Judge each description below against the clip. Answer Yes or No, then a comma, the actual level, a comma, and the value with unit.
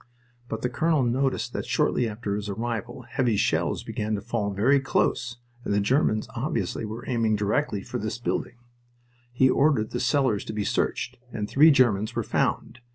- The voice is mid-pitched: No, low, 120 Hz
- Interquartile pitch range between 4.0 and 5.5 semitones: No, average, 3.3 semitones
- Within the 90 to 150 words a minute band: No, average, 175 wpm